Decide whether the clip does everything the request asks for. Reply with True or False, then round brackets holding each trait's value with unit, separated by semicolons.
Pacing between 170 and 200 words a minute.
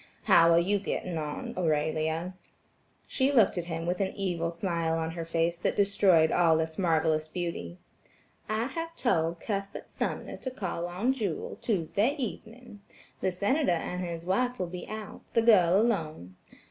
False (160 wpm)